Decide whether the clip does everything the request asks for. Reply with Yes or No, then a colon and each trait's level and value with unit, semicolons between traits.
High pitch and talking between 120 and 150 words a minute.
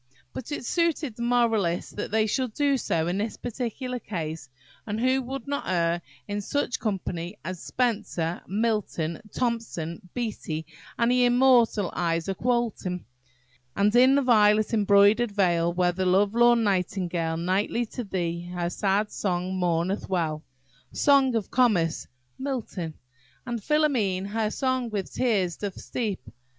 Yes: high, 210 Hz; average, 140 wpm